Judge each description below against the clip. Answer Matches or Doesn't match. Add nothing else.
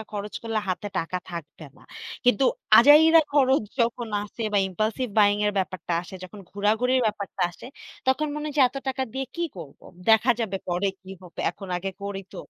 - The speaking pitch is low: Doesn't match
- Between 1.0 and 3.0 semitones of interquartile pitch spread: Doesn't match